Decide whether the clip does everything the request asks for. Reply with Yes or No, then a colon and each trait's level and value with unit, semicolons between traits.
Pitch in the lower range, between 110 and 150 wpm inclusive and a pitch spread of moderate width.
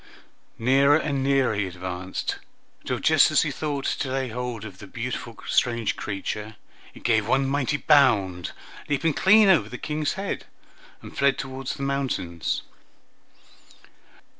Yes: low, 130 Hz; average, 140 wpm; average, 4.6 semitones